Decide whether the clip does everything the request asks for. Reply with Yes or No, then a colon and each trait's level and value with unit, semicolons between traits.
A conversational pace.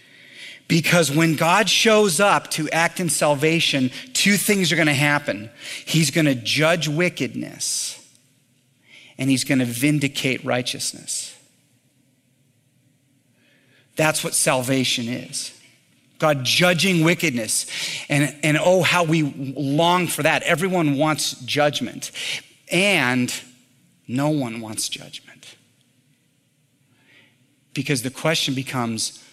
No: slow, 110 wpm